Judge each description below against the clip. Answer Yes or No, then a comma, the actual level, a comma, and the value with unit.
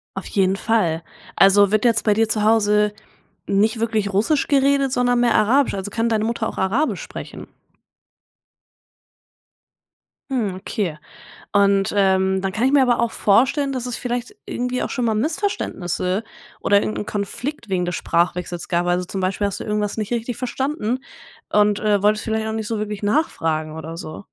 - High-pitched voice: Yes, high, 210 Hz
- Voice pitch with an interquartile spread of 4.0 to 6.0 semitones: No, average, 3.6 semitones